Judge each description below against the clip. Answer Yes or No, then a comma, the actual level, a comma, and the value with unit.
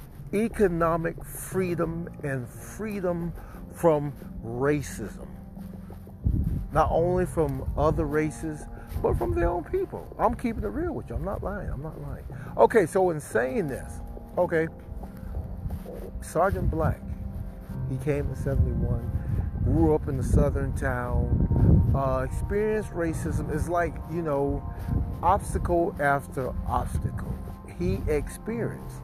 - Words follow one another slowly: Yes, slow, 115 wpm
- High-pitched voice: No, medium, 140 Hz